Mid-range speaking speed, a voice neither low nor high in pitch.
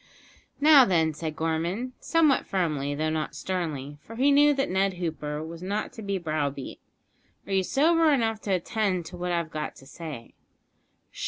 Yes: average, 170 wpm; medium, 180 Hz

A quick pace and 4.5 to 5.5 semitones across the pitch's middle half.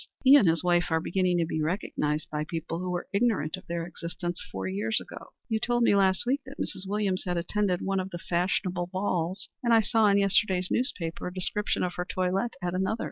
No: fast, 220 wpm; average, 2.8 semitones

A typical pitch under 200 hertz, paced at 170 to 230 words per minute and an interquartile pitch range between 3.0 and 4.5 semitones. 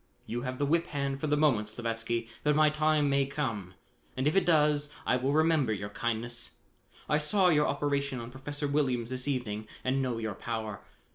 Yes: low, 135 Hz; average, 195 wpm; average, 4.1 semitones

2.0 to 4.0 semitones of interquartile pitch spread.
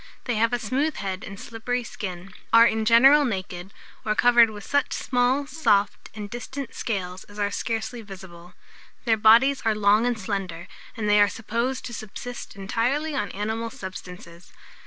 Yes: average, 3.5 semitones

